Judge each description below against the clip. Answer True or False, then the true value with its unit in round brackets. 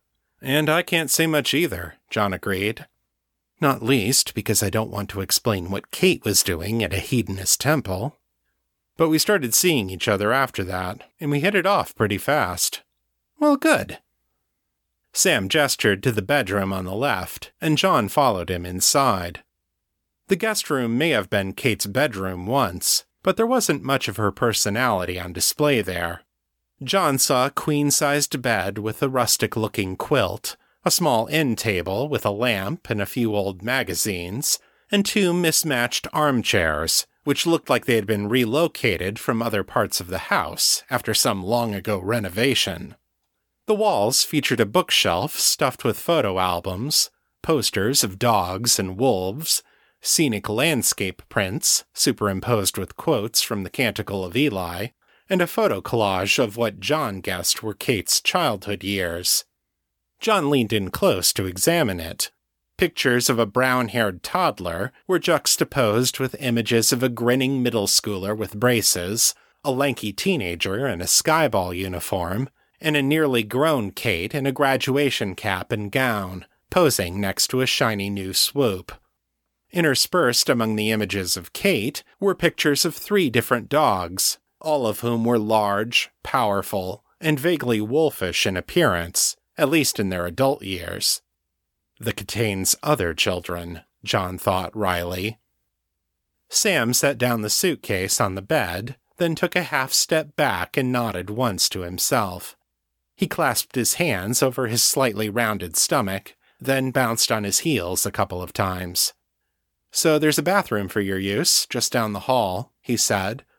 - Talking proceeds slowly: False (155 wpm)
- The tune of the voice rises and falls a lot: True (6.4 semitones)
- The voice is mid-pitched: False (115 Hz)